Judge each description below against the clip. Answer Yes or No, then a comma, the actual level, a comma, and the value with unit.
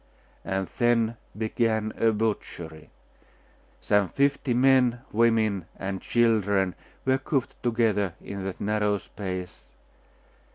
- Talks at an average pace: No, slow, 100 wpm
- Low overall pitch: Yes, low, 110 Hz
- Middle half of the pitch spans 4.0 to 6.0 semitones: No, average, 3.4 semitones